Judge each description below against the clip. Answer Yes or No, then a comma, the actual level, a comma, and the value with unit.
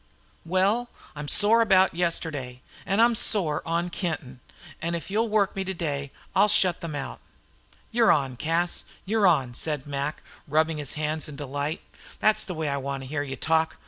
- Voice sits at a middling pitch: Yes, medium, 160 Hz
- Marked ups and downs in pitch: No, average, 4.9 semitones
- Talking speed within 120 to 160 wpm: No, average, 180 wpm